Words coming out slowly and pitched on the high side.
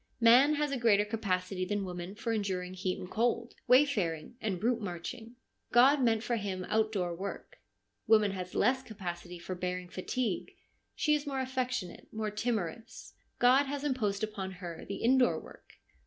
No: average, 160 wpm; high, 215 Hz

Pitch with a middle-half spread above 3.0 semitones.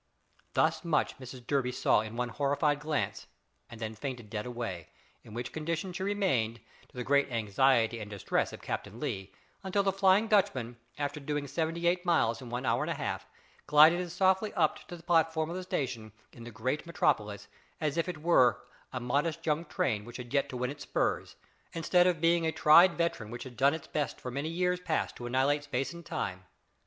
Yes: wide, 5.6 semitones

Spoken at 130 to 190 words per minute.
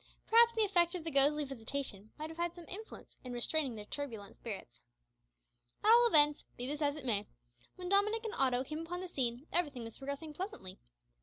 No: average, 200 wpm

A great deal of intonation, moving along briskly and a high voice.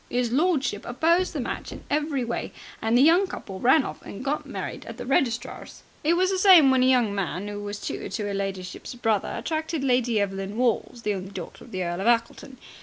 Yes: wide, 6.2 semitones; fast, 220 wpm; high, 245 Hz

